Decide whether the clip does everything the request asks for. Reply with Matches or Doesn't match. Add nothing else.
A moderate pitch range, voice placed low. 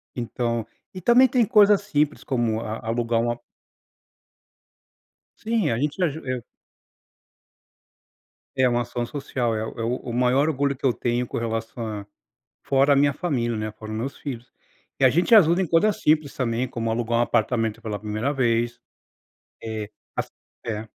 Matches